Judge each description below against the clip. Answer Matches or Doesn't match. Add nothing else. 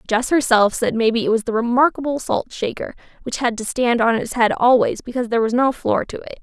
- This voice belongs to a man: Doesn't match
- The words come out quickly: Matches